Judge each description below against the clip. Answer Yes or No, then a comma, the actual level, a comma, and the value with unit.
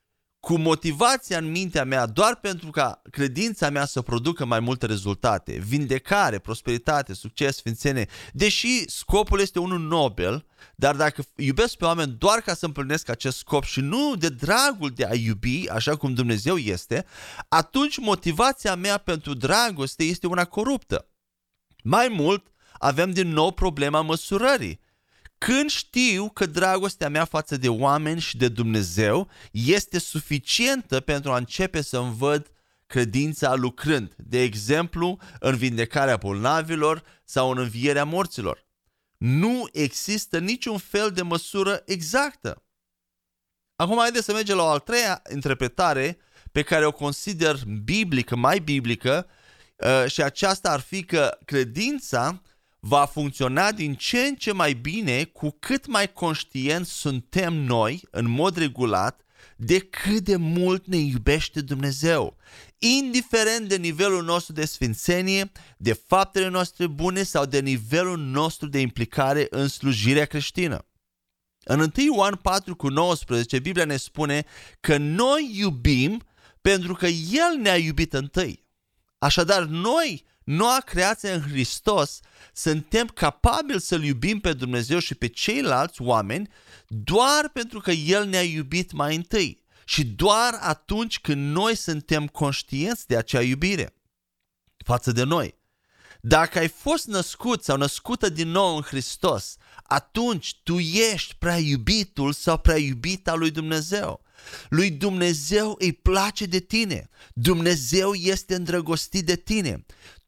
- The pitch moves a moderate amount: No, wide, 5.9 semitones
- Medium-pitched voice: Yes, medium, 160 Hz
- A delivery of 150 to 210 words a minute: No, average, 135 wpm